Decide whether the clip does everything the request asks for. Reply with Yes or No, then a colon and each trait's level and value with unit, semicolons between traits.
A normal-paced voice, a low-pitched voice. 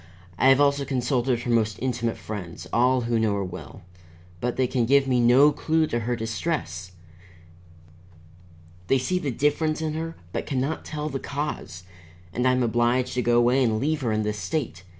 Yes: average, 190 wpm; low, 125 Hz